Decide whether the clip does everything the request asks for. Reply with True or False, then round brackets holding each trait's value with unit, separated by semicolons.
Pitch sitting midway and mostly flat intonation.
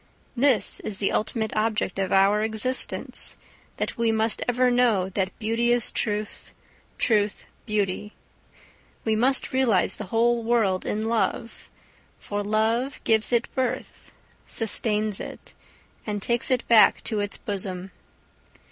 False (220 Hz; 2.3 semitones)